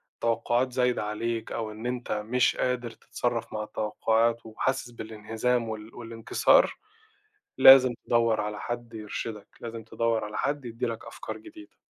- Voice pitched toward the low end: Yes, low, 115 Hz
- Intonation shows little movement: Yes, narrow, 1.9 semitones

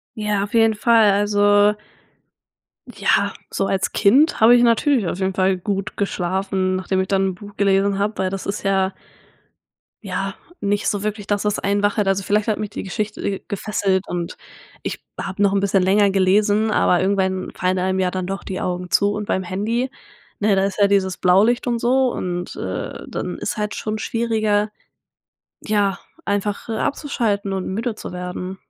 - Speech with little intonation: Yes, narrow, 1.9 semitones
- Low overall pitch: No, high, 200 Hz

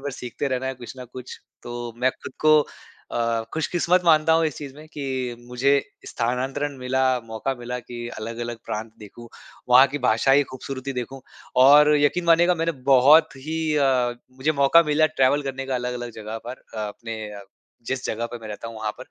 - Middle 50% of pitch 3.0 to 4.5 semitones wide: Yes, average, 3.3 semitones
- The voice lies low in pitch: Yes, low, 130 Hz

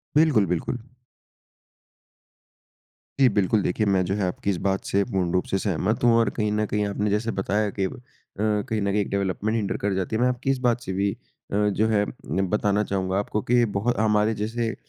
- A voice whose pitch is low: Yes, low, 105 Hz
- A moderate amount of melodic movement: No, narrow, 2.2 semitones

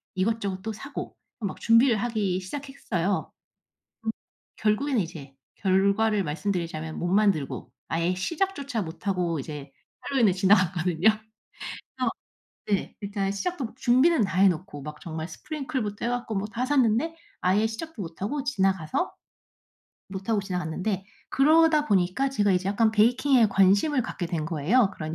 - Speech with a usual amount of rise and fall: Yes, average, 5.0 semitones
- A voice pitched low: No, high, 200 Hz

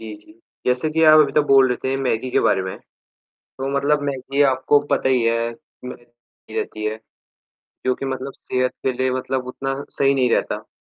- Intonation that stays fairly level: Yes, narrow, 1.6 semitones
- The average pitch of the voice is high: No, low, 130 Hz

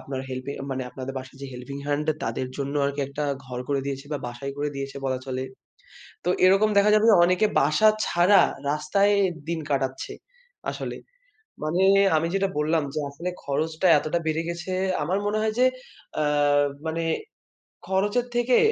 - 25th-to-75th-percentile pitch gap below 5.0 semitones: No, average, 5.3 semitones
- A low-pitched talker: No, medium, 150 Hz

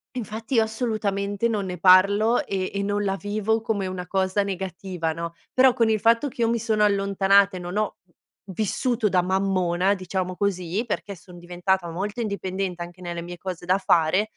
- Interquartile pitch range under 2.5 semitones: No, average, 2.8 semitones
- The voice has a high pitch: Yes, high, 195 Hz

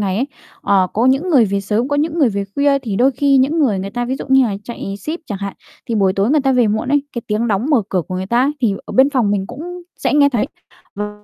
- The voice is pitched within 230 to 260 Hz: Yes, high, 240 Hz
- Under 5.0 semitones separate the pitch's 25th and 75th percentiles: No, wide, 5.5 semitones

